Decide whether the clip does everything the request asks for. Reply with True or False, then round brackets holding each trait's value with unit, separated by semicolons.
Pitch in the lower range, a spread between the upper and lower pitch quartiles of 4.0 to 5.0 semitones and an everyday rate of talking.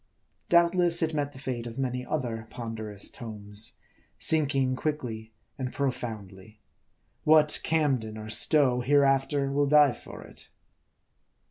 False (130 Hz; 4.5 semitones; 120 wpm)